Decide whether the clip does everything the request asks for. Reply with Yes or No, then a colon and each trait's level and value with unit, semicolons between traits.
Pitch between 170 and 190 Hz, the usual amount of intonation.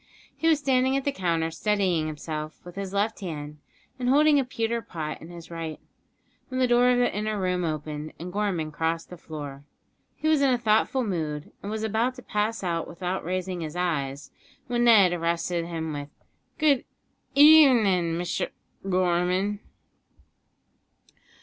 No: medium, 185 Hz; wide, 6.2 semitones